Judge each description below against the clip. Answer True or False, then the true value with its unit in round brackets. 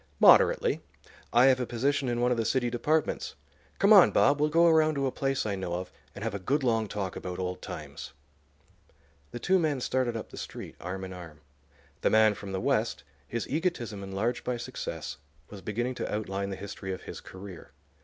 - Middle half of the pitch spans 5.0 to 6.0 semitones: True (5.6 semitones)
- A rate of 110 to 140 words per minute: False (205 wpm)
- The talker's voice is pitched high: False (115 Hz)